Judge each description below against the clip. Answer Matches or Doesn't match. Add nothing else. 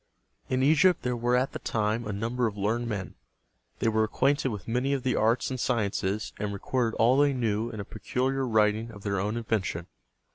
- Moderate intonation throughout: Matches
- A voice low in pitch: Matches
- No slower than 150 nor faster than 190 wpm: Doesn't match